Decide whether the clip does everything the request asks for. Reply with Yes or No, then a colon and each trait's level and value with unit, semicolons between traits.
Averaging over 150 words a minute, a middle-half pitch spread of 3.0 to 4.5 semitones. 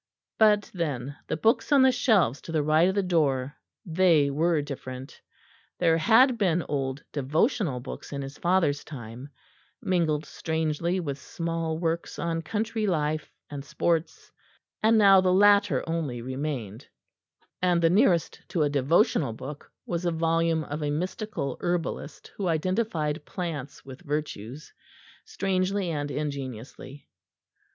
No: slow, 135 wpm; average, 4.2 semitones